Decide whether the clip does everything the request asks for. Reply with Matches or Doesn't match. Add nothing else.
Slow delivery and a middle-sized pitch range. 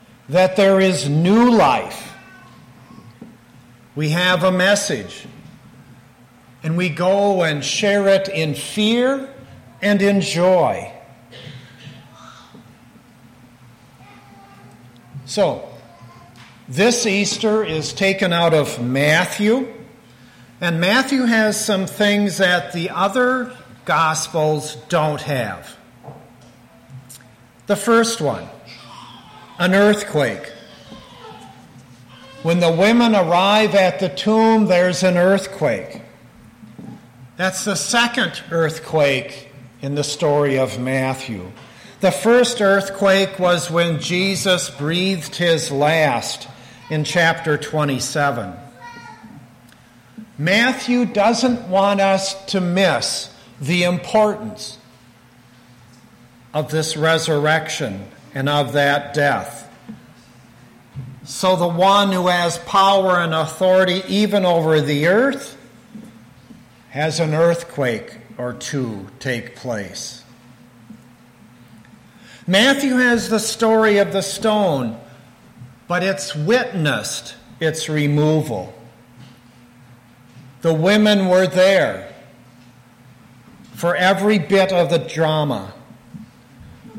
Doesn't match